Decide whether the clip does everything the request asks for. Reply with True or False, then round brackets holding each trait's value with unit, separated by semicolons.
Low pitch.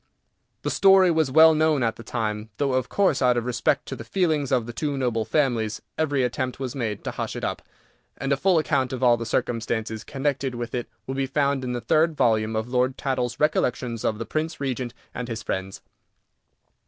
True (130 Hz)